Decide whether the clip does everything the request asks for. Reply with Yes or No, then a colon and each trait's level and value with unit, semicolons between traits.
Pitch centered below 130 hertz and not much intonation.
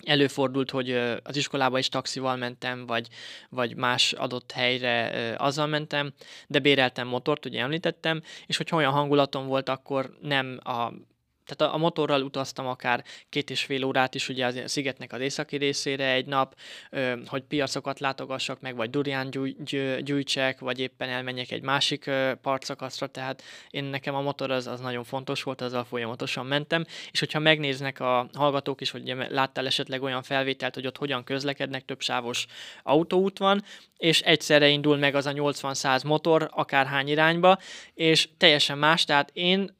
No: low, 135 Hz; narrow, 1.9 semitones